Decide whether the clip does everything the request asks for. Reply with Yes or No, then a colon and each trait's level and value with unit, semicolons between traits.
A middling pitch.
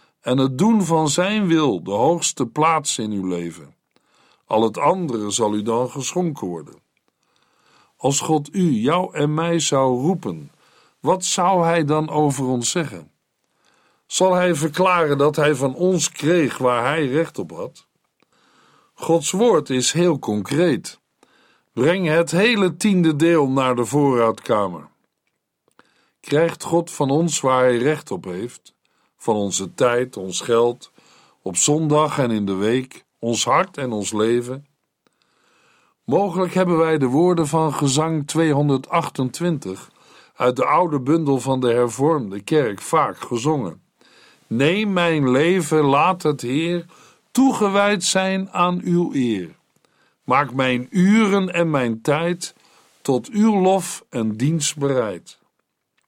Yes: medium, 155 Hz